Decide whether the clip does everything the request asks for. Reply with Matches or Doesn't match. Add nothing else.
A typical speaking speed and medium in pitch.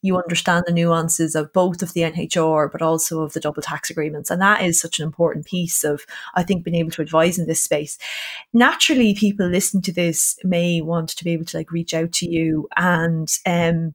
Doesn't match